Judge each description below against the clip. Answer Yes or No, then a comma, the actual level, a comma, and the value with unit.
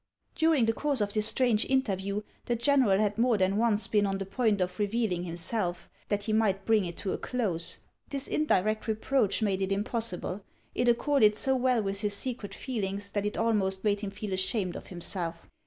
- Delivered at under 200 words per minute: No, fast, 205 wpm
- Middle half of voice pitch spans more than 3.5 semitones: No, average, 3.1 semitones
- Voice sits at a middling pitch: No, high, 210 Hz